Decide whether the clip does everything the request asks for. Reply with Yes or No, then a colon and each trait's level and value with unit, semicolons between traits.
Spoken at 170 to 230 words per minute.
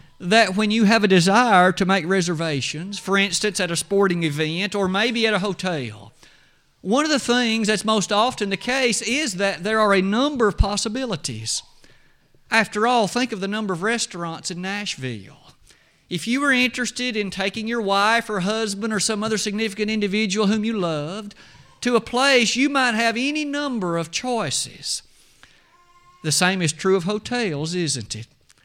Yes: average, 175 wpm